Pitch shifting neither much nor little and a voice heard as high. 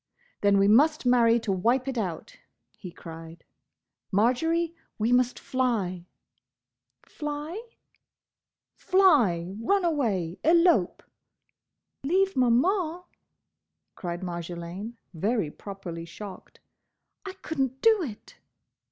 No: wide, 8.9 semitones; high, 235 Hz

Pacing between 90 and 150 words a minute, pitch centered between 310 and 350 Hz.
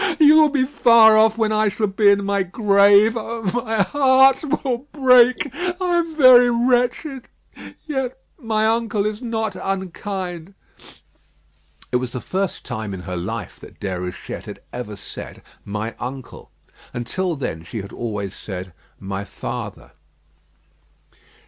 No: average, 140 wpm; high, 215 Hz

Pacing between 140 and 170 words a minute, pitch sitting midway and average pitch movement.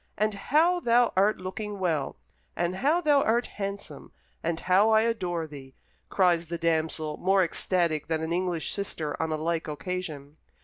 Yes: average, 165 wpm; medium, 180 Hz; average, 4.5 semitones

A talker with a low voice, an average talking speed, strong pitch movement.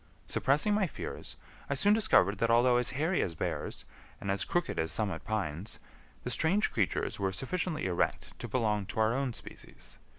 Yes: low, 115 Hz; average, 175 wpm; wide, 7.6 semitones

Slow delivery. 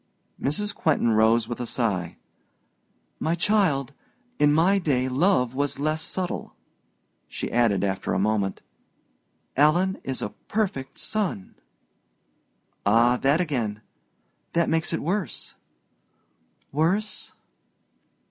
Yes: slow, 110 wpm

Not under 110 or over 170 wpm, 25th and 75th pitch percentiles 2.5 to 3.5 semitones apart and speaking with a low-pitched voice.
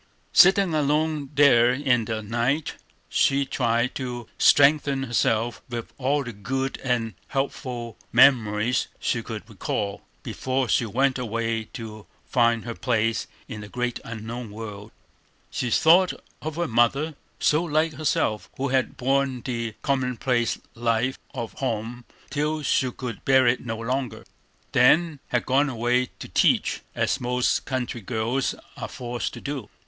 Yes: average, 145 wpm; average, 3.1 semitones; low, 125 Hz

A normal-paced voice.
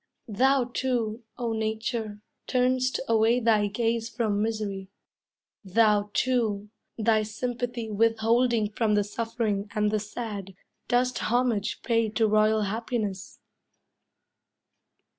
No: slow, 105 wpm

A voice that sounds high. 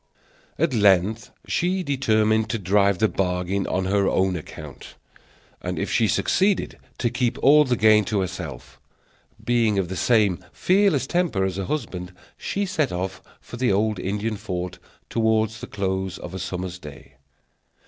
No: low, 105 Hz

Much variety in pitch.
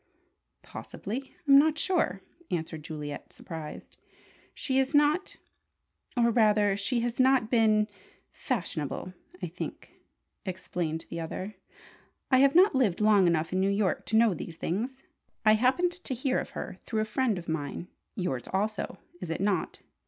Yes: wide, 6.5 semitones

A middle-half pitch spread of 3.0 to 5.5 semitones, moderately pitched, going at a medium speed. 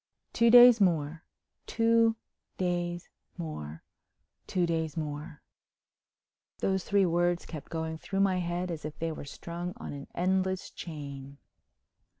No: average, 3.3 semitones; medium, 175 Hz; slow, 115 wpm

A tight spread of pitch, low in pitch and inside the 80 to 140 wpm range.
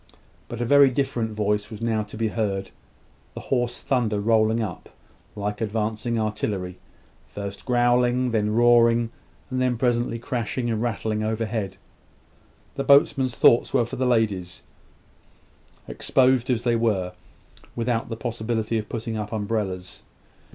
Yes: narrow, 2.2 semitones; low, 115 Hz; slow, 135 wpm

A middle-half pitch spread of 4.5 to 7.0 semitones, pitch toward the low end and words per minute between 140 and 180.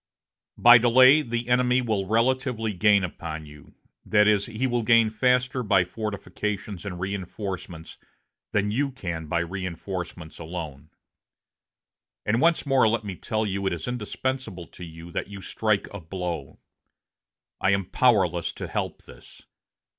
Yes: average, 4.9 semitones; low, 105 Hz; average, 145 wpm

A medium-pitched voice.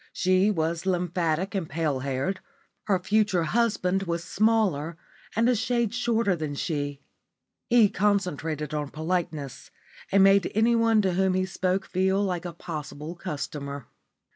Yes: medium, 180 Hz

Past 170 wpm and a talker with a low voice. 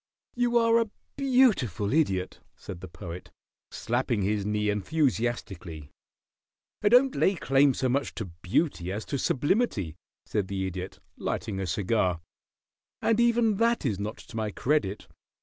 No: average, 145 wpm; low, 115 Hz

